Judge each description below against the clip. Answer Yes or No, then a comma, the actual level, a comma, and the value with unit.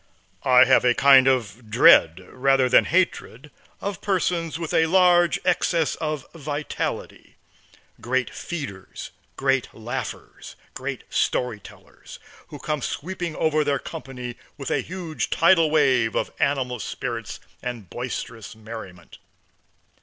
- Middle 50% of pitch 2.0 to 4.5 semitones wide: No, average, 5.0 semitones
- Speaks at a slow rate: Yes, slow, 125 wpm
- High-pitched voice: No, low, 135 Hz